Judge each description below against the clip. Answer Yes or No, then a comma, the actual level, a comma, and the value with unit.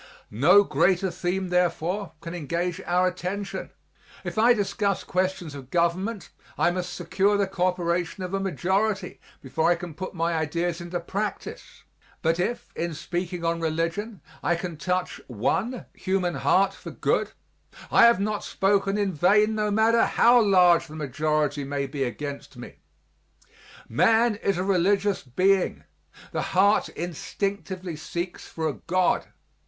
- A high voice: No, medium, 180 Hz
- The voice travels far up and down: No, average, 2.8 semitones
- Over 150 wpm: No, average, 145 wpm